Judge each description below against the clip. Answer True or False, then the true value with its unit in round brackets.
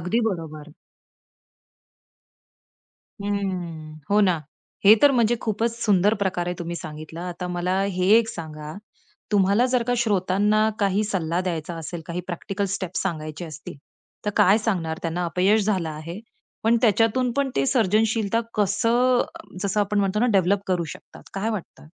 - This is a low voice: False (190 Hz)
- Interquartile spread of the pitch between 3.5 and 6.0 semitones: True (3.9 semitones)